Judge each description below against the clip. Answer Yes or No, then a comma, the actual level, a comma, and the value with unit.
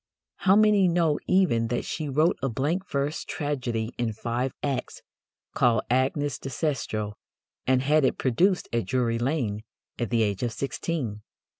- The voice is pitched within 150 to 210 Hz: No, low, 130 Hz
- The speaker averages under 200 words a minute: Yes, average, 155 wpm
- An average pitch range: Yes, average, 4.8 semitones